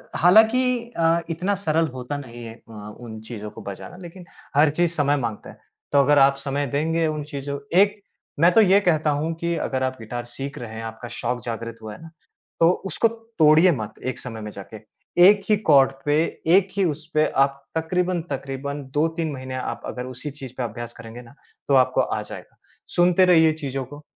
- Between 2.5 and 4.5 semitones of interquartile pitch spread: No, average, 5.1 semitones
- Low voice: No, medium, 145 Hz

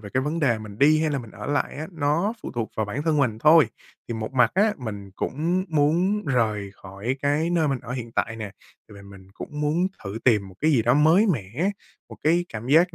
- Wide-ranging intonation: Yes, wide, 6.3 semitones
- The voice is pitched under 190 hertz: Yes, medium, 140 Hz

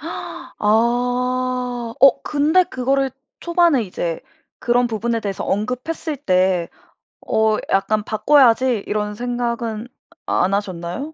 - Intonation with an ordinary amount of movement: Yes, average, 3.6 semitones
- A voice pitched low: No, high, 240 Hz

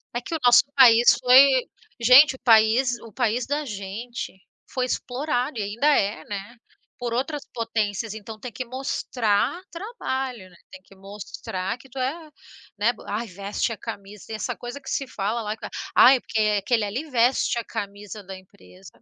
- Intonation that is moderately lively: Yes, average, 3.9 semitones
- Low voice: No, high, 235 Hz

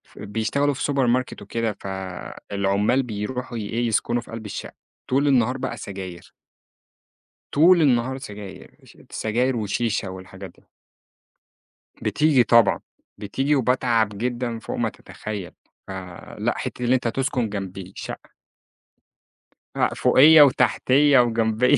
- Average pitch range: Yes, average, 4.2 semitones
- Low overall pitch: Yes, low, 115 Hz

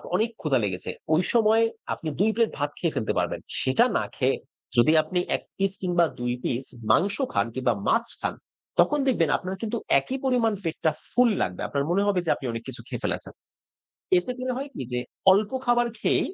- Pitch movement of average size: No, wide, 8.0 semitones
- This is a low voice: No, medium, 185 Hz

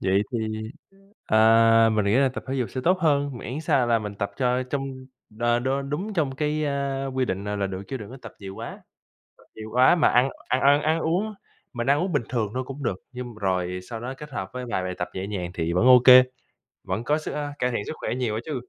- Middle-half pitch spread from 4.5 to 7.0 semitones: Yes, average, 4.9 semitones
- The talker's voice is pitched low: Yes, low, 125 Hz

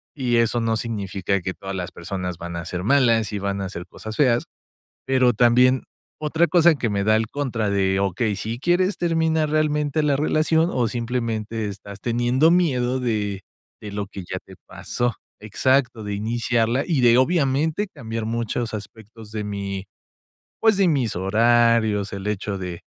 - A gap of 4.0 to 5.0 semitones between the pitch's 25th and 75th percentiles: Yes, average, 4.6 semitones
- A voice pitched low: Yes, low, 115 Hz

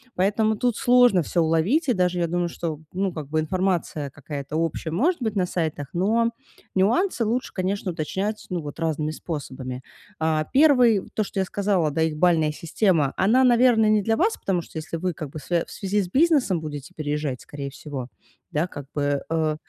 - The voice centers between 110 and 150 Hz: No, medium, 175 Hz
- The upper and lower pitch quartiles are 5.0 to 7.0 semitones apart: Yes, wide, 5.6 semitones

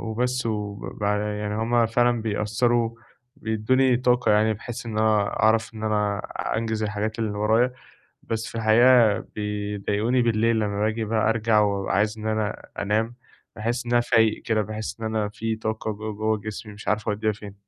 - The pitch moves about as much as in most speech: No, narrow, 1.5 semitones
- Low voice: Yes, low, 110 Hz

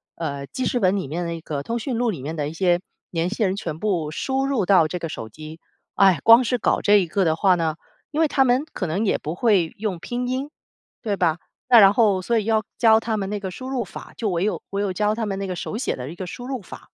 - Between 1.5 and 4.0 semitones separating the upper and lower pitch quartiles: No, wide, 5.4 semitones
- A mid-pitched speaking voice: No, high, 195 Hz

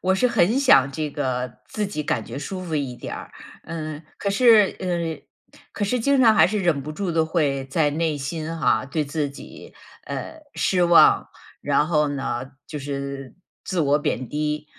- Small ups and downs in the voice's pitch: No, average, 4.8 semitones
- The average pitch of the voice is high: No, medium, 155 Hz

